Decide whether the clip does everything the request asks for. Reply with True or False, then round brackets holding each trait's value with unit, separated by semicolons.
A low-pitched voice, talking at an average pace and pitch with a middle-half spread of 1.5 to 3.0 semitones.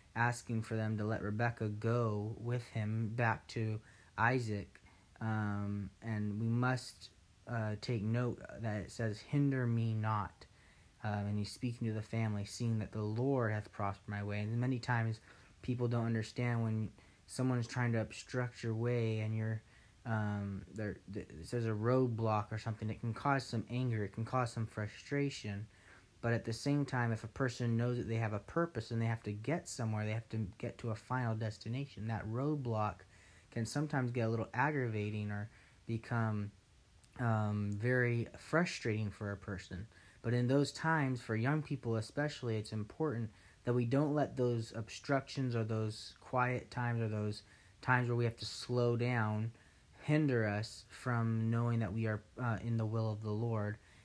True (115 Hz; 180 wpm; 2.5 semitones)